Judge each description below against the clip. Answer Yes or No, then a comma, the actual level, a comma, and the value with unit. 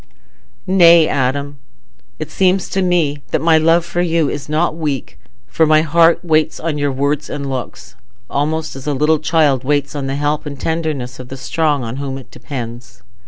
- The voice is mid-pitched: Yes, medium, 150 Hz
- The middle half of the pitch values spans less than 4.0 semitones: Yes, average, 2.9 semitones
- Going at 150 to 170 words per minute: No, average, 185 wpm